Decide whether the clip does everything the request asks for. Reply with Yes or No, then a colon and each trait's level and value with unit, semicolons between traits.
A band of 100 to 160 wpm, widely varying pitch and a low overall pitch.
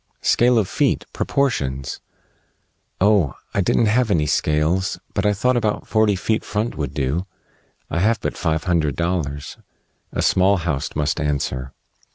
Yes: average, 150 wpm; wide, 6.2 semitones; very low, 90 Hz